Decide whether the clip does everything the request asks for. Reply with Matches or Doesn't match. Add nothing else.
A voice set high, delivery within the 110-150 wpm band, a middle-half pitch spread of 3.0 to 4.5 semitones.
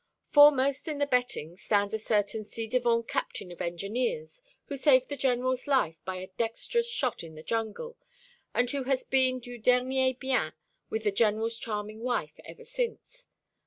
Doesn't match